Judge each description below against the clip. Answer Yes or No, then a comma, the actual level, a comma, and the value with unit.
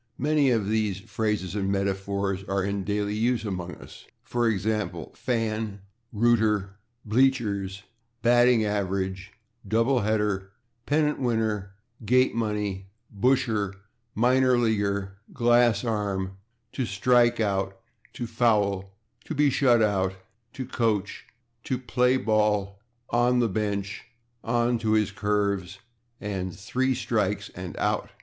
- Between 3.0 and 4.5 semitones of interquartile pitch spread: Yes, average, 3.3 semitones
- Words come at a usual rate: No, slow, 120 wpm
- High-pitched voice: No, low, 105 Hz